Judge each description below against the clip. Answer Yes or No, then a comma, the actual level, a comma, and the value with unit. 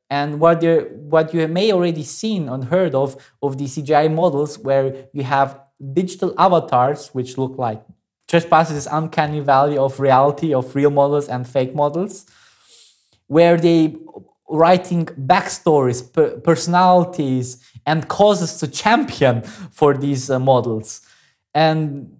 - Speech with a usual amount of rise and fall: Yes, average, 3.7 semitones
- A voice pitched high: No, medium, 145 Hz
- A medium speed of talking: No, slow, 130 wpm